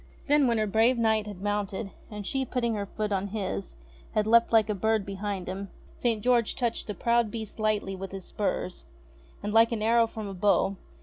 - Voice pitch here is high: Yes, high, 215 Hz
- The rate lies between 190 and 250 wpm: Yes, fast, 205 wpm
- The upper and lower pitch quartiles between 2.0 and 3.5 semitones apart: Yes, narrow, 2.5 semitones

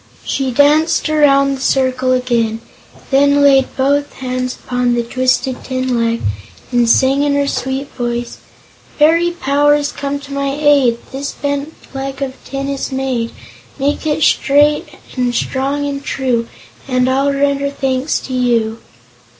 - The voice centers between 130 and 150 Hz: No, very high, 270 Hz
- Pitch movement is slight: Yes, narrow, 1.9 semitones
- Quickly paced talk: No, average, 150 wpm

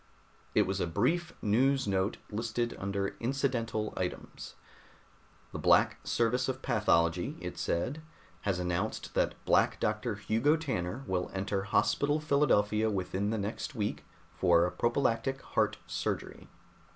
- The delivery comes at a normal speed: No, slow, 125 wpm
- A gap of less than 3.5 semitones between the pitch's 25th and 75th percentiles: No, average, 4.9 semitones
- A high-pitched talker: No, low, 110 Hz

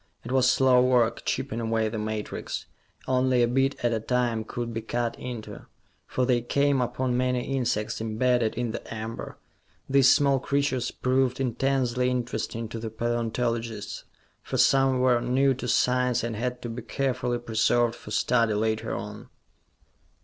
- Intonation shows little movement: Yes, narrow, 2.0 semitones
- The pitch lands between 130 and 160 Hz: No, low, 120 Hz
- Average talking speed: Yes, average, 155 wpm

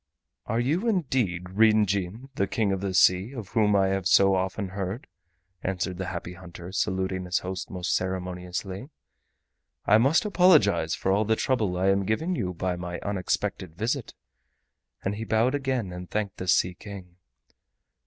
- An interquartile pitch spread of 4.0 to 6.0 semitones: No, average, 3.4 semitones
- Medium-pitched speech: No, very low, 95 Hz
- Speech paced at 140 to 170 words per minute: Yes, average, 165 wpm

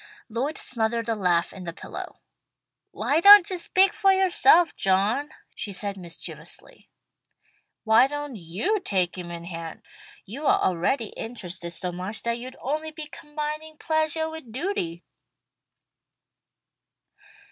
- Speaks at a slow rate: Yes, slow, 130 wpm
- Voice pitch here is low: No, high, 235 Hz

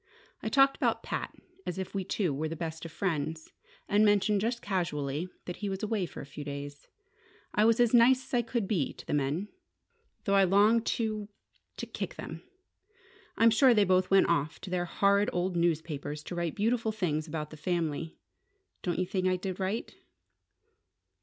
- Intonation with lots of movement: No, average, 4.7 semitones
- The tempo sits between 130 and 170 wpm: No, average, 190 wpm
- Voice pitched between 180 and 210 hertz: Yes, medium, 185 Hz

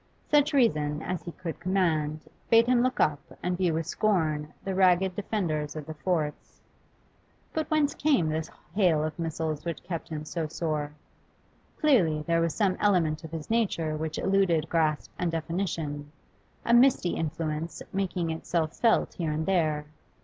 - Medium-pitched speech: Yes, medium, 165 Hz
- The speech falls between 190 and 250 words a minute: No, average, 160 wpm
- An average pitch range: Yes, average, 3.7 semitones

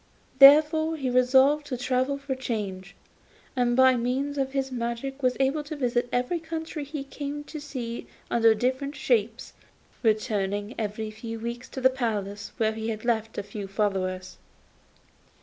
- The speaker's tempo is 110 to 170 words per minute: Yes, average, 160 wpm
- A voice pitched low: No, very high, 250 Hz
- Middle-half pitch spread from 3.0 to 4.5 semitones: Yes, average, 3.9 semitones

